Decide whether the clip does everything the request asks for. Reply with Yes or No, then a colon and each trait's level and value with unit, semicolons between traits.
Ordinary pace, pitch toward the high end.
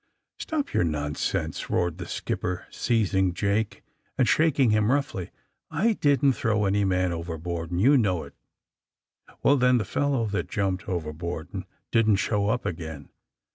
No: average, 155 wpm; low, 100 Hz